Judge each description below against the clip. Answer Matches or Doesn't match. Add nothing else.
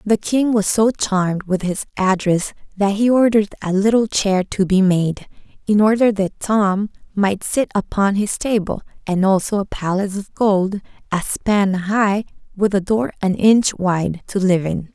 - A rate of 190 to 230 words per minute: Doesn't match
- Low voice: Doesn't match